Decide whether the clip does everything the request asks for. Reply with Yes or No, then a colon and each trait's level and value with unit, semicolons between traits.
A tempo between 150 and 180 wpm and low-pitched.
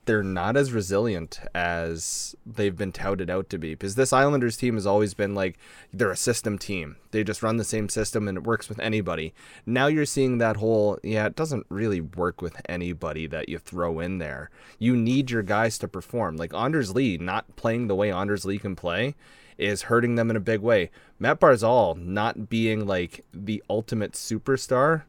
No: average, 200 wpm; low, 105 Hz